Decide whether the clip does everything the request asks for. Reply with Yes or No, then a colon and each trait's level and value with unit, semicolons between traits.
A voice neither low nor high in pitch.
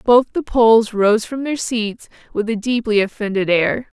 No: high, 225 Hz